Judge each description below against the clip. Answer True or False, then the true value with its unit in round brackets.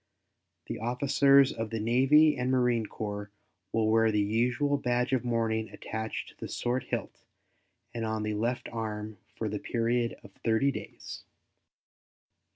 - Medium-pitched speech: False (115 Hz)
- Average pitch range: False (2.2 semitones)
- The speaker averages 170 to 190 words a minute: False (150 wpm)